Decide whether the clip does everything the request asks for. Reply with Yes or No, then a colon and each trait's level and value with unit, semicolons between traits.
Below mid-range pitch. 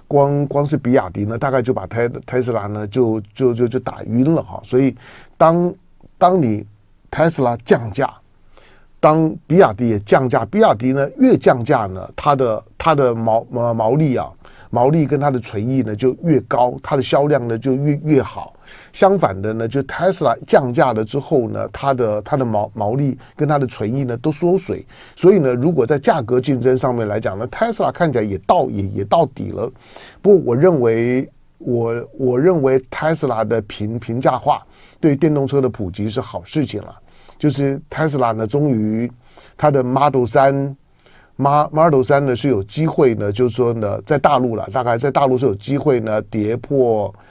Yes: low, 130 Hz